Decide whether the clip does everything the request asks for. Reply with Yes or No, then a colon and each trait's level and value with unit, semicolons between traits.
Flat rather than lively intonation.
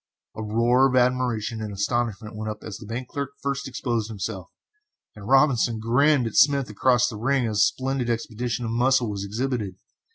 No: average, 3.1 semitones